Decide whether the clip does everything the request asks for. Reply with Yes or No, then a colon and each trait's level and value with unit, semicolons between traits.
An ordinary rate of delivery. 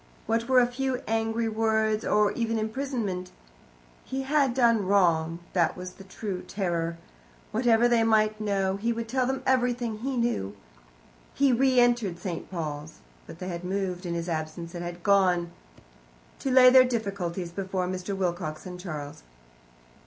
Yes: average, 160 wpm